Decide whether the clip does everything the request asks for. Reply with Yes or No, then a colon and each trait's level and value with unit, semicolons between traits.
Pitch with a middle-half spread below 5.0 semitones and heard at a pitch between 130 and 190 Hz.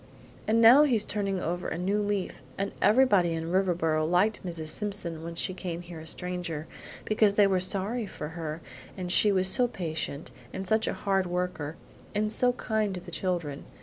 Yes: average, 3.6 semitones; medium, 185 Hz